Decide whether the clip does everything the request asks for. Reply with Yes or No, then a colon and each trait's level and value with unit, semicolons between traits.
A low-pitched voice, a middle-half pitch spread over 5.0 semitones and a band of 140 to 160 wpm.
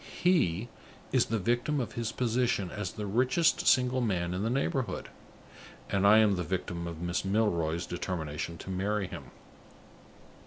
Yes: low, 105 Hz; wide, 5.4 semitones; average, 155 wpm